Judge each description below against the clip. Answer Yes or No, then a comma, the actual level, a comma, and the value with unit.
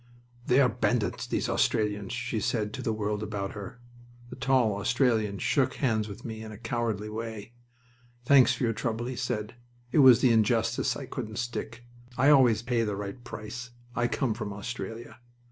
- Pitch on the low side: Yes, low, 115 Hz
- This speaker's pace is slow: No, average, 180 wpm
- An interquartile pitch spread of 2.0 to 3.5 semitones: Yes, narrow, 2.5 semitones